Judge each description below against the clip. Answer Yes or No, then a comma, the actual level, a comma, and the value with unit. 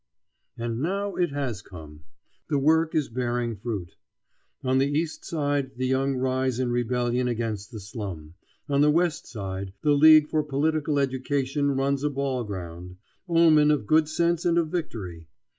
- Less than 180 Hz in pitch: Yes, low, 135 Hz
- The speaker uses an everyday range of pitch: Yes, average, 4.7 semitones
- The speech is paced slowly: No, average, 160 wpm